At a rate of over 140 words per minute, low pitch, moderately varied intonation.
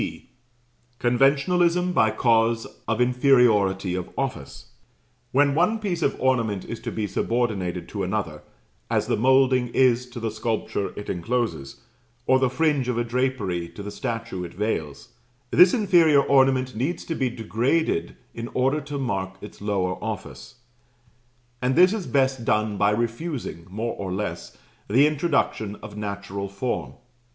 Yes: average, 150 wpm; low, 120 Hz; average, 4.7 semitones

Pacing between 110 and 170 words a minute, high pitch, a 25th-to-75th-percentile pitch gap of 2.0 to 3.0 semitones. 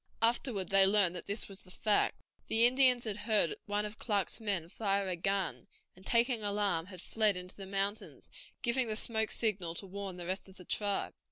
No: average, 200 wpm; high, 200 Hz; narrow, 2.6 semitones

